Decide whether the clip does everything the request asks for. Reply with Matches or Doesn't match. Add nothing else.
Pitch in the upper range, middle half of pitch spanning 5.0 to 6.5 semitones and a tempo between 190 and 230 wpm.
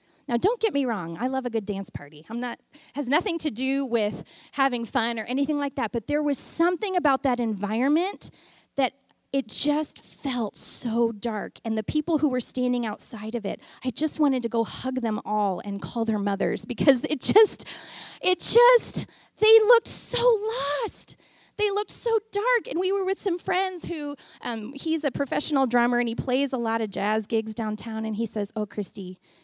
Matches